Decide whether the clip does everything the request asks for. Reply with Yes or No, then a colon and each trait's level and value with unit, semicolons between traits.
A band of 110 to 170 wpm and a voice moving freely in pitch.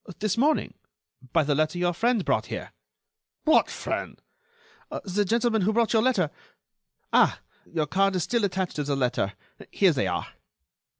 Yes: average, 160 wpm; wide, 6.4 semitones